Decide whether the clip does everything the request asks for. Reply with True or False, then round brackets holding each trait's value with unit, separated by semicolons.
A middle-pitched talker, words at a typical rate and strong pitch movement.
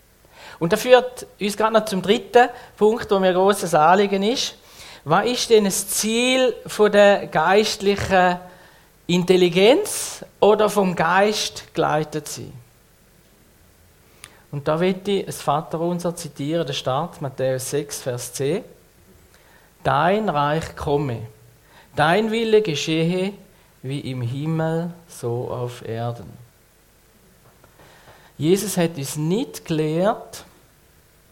False (175 Hz; 110 wpm; 6.0 semitones)